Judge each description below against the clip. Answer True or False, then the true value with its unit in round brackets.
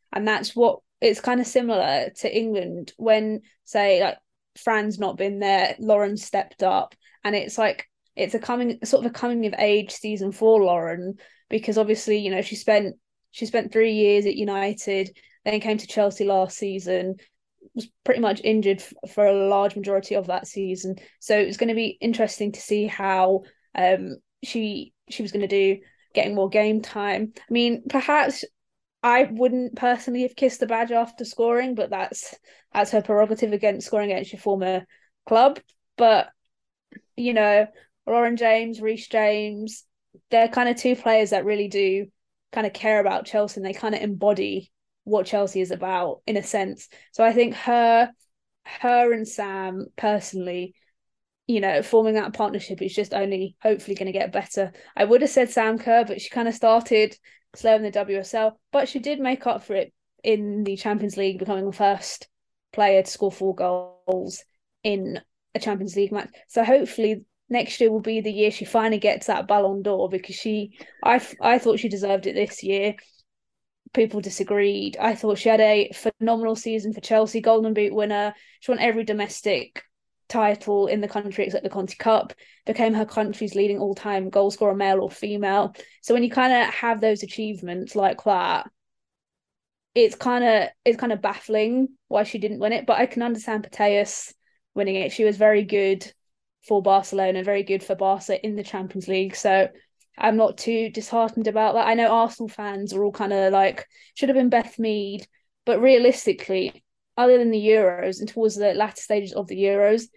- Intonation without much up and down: True (2.3 semitones)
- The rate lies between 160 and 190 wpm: True (185 wpm)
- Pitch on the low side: False (215 Hz)